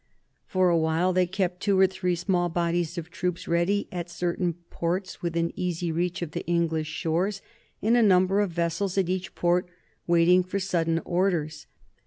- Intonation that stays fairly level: Yes, narrow, 1.7 semitones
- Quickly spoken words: No, average, 170 wpm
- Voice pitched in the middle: Yes, medium, 175 Hz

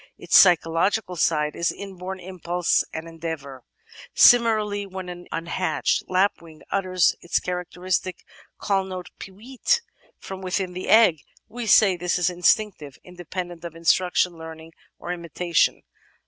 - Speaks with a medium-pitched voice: Yes, medium, 180 Hz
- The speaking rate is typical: No, slow, 130 wpm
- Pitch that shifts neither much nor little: No, narrow, 2.3 semitones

